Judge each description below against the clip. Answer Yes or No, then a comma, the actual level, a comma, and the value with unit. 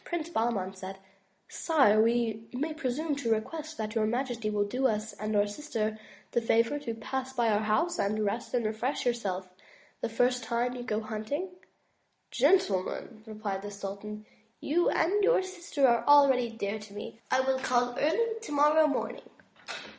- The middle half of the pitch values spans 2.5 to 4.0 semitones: No, average, 5.1 semitones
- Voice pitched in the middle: No, high, 235 Hz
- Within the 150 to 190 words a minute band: Yes, average, 165 wpm